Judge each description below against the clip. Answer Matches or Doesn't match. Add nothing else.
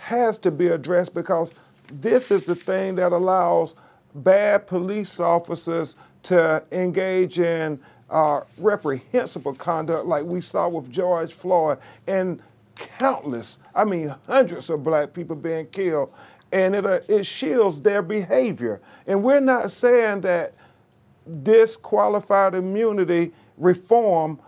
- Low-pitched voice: Doesn't match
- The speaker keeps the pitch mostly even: Doesn't match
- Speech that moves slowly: Matches